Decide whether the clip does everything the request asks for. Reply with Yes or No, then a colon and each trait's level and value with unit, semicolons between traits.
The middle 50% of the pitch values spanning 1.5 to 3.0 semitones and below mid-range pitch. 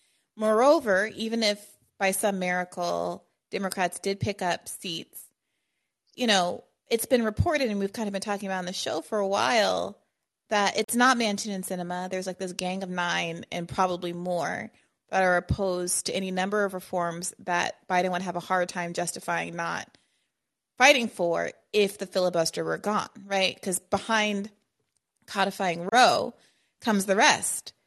No: average, 2.7 semitones; high, 195 Hz